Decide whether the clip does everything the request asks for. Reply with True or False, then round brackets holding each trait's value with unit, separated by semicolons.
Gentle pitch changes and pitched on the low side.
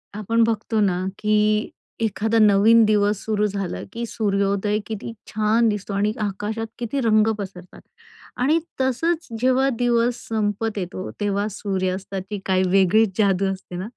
False (2.3 semitones; 210 Hz)